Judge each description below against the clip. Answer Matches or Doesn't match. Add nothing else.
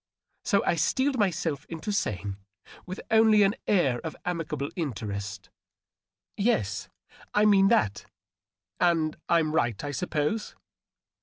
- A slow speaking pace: Matches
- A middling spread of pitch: Doesn't match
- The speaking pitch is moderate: Matches